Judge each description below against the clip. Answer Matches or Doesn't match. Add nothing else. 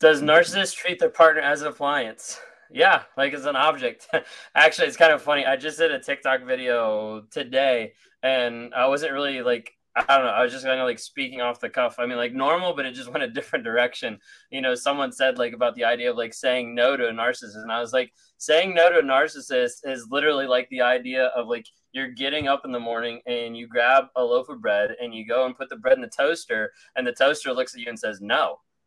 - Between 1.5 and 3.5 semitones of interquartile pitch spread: Matches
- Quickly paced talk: Matches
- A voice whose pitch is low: Matches